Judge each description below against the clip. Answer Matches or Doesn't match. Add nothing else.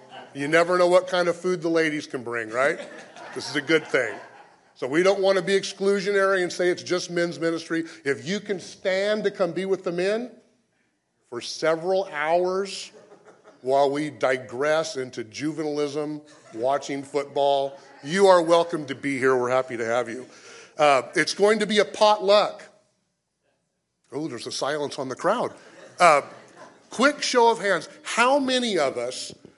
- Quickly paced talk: Doesn't match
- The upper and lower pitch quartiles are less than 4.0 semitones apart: Doesn't match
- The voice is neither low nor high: Matches